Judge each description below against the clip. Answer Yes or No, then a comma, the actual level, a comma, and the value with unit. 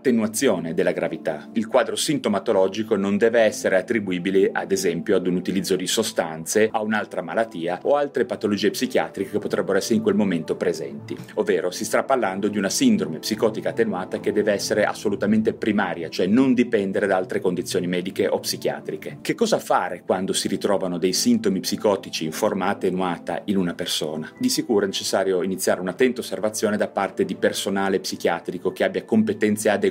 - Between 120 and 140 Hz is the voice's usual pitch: No, low, 105 Hz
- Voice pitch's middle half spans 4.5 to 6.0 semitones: Yes, wide, 5.4 semitones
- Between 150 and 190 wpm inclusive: Yes, fast, 170 wpm